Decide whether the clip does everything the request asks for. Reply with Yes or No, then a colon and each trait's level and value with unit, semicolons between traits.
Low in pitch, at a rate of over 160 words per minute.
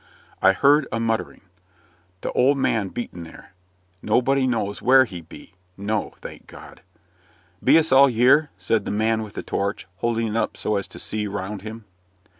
Yes: low, 110 Hz; average, 175 wpm